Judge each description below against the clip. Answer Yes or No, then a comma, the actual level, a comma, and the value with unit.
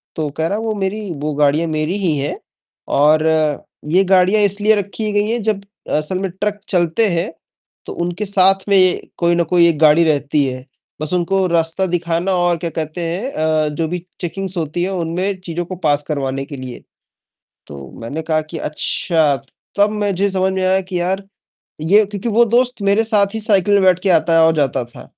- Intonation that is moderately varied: Yes, average, 3.9 semitones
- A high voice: No, medium, 175 Hz